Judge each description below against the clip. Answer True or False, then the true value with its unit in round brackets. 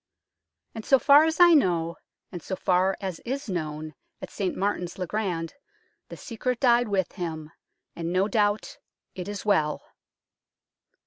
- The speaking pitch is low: False (190 Hz)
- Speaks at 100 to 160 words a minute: True (150 wpm)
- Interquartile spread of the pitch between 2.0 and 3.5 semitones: False (4.9 semitones)